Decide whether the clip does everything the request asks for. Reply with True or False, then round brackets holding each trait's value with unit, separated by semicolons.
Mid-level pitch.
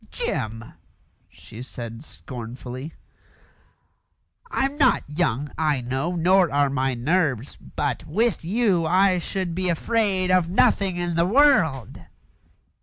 True (165 Hz)